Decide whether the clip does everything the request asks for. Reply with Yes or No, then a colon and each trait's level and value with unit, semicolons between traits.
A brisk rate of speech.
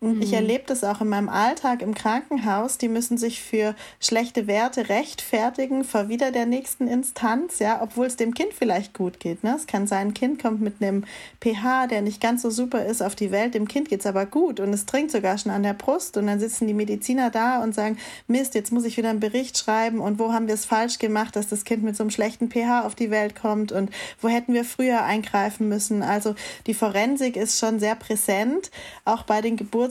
Yes: fast, 230 wpm